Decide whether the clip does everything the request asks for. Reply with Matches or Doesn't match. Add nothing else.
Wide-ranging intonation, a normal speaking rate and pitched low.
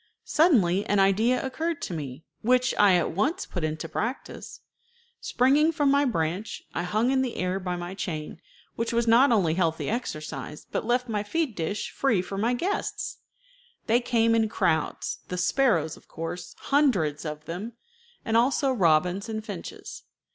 Doesn't match